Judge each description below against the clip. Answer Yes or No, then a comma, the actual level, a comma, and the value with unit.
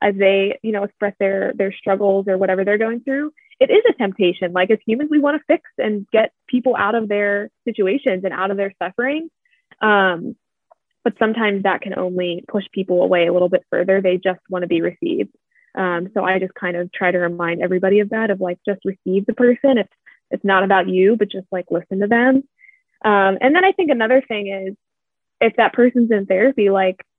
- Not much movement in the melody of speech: No, average, 4.6 semitones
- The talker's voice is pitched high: Yes, high, 200 Hz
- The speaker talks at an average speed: No, fast, 215 wpm